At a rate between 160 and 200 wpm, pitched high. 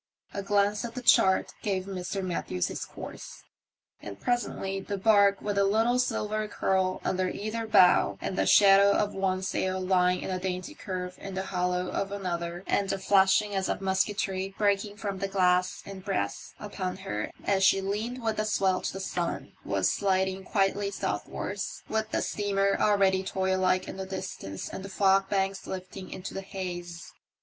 Yes: average, 175 wpm; high, 195 Hz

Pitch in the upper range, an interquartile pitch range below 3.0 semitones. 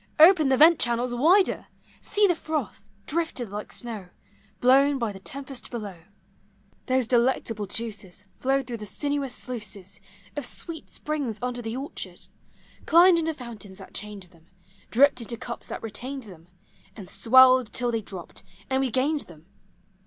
No: high, 245 Hz; average, 4.8 semitones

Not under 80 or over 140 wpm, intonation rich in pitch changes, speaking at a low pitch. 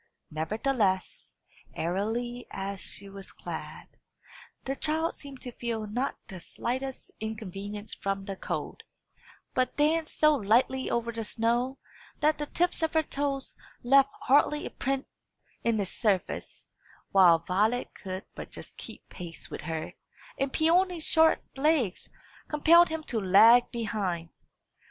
No: slow, 135 wpm; wide, 5.9 semitones; high, 235 Hz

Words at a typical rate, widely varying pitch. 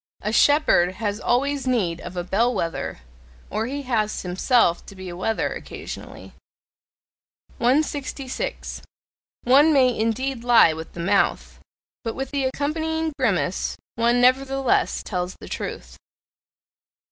No: slow, 125 wpm; wide, 5.8 semitones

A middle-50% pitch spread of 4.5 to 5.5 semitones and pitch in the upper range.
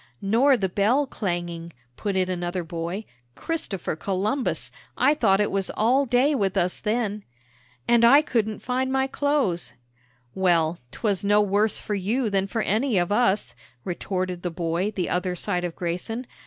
Yes: average, 4.9 semitones; high, 200 Hz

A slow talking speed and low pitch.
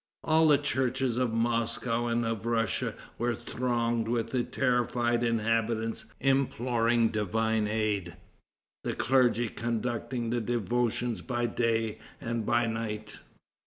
Yes: slow, 120 wpm; low, 115 Hz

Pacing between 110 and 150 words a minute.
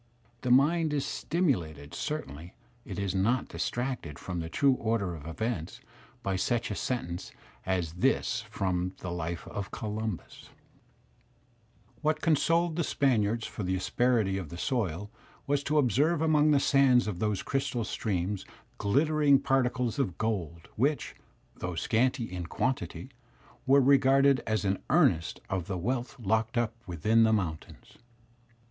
Yes: average, 140 wpm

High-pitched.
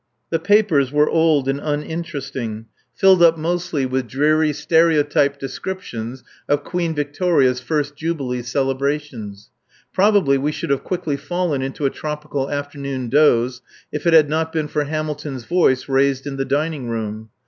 No: medium, 145 Hz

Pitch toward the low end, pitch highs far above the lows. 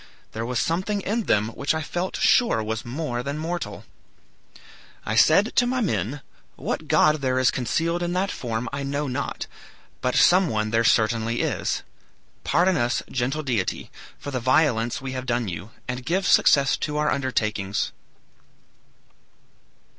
Yes: low, 130 Hz; wide, 5.7 semitones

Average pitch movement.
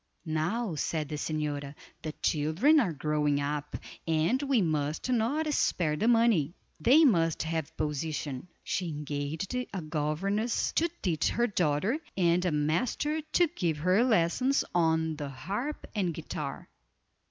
No: wide, 7.0 semitones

